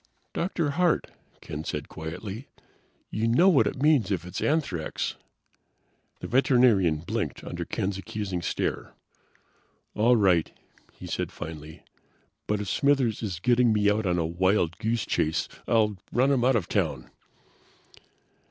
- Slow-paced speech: No, average, 145 wpm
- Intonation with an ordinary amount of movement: No, wide, 6.0 semitones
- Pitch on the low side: Yes, low, 105 Hz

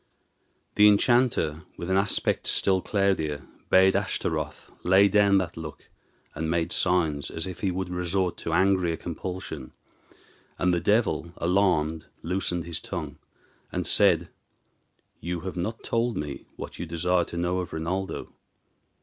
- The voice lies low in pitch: Yes, very low, 90 Hz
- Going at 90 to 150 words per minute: Yes, average, 140 wpm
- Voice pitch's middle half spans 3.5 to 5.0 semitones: No, average, 2.8 semitones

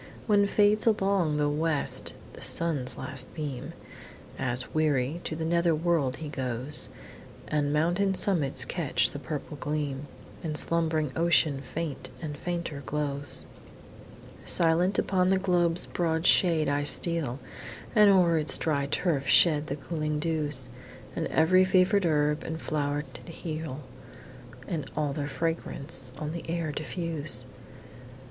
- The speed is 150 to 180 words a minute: No, slow, 135 wpm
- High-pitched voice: No, medium, 155 Hz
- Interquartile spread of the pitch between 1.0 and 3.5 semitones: Yes, average, 2.9 semitones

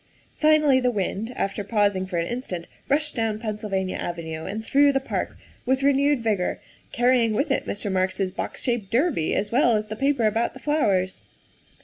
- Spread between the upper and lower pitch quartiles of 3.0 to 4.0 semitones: No, wide, 5.4 semitones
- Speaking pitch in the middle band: No, high, 220 Hz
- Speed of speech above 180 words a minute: Yes, average, 190 wpm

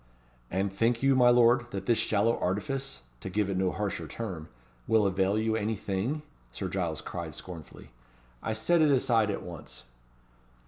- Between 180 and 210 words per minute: No, average, 170 wpm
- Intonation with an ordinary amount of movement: Yes, average, 4.1 semitones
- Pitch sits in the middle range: No, low, 110 Hz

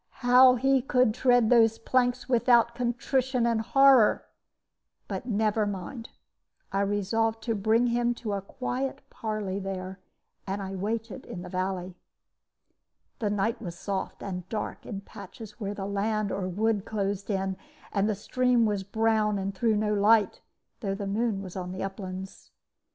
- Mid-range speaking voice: No, high, 215 Hz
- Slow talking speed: No, average, 155 wpm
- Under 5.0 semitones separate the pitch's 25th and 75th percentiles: Yes, average, 3.2 semitones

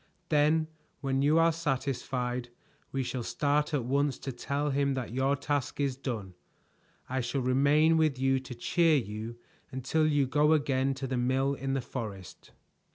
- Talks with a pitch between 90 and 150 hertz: Yes, low, 135 Hz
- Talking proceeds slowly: No, average, 165 wpm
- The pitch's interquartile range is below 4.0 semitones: Yes, narrow, 2.4 semitones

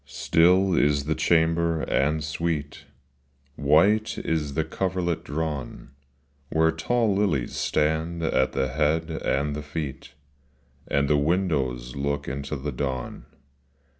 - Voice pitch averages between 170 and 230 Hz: No, very low, 75 Hz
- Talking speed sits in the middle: No, slow, 120 wpm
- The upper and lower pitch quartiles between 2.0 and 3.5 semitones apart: Yes, average, 2.8 semitones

